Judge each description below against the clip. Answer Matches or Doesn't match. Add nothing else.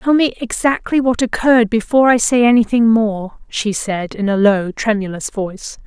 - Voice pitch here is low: Doesn't match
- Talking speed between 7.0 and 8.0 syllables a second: Doesn't match